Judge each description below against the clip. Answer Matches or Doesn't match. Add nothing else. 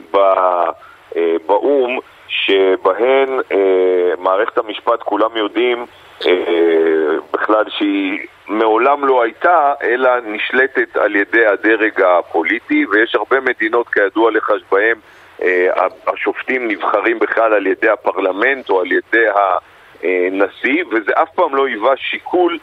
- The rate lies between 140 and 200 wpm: Doesn't match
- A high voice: Matches